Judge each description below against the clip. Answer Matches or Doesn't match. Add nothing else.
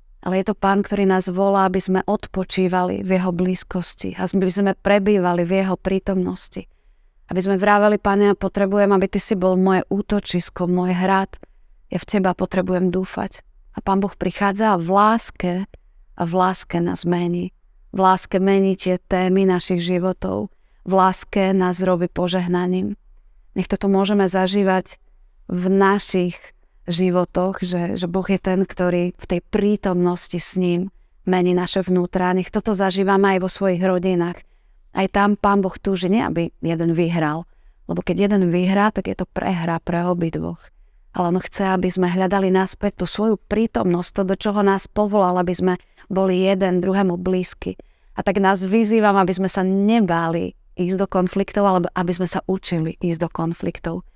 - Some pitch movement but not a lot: Doesn't match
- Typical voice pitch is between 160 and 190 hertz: Matches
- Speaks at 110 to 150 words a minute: Doesn't match